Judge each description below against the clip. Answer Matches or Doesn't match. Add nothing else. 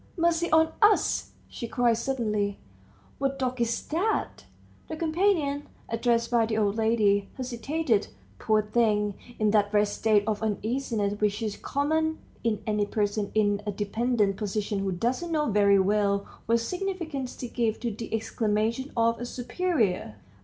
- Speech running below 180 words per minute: Matches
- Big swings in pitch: Doesn't match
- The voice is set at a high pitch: Matches